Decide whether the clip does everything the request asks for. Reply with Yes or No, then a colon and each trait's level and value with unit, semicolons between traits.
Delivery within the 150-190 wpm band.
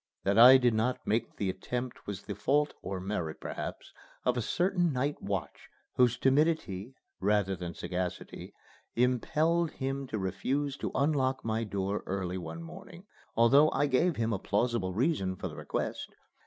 Yes: average, 160 wpm